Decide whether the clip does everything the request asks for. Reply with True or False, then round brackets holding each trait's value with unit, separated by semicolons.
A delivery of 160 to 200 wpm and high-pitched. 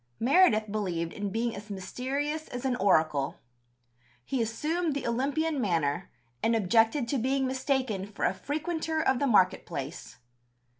False (145 wpm; 235 Hz)